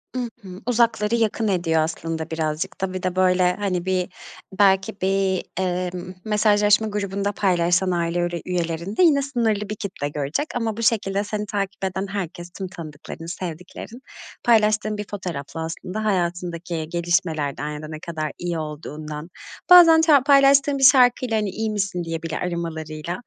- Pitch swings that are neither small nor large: Yes, average, 4.0 semitones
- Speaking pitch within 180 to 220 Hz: Yes, medium, 185 Hz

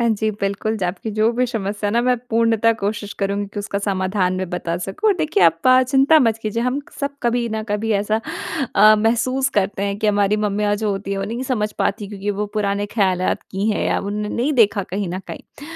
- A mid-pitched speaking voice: No, high, 210 Hz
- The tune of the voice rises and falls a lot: No, narrow, 2.4 semitones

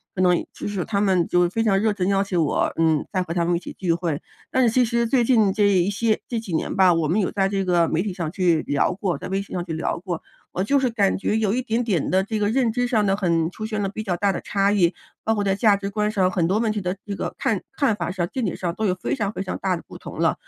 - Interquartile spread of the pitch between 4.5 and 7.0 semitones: No, average, 3.3 semitones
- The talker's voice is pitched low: No, high, 195 Hz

